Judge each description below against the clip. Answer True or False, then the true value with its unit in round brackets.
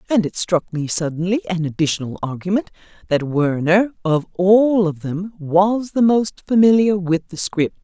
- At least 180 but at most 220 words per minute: False (160 wpm)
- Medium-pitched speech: True (180 Hz)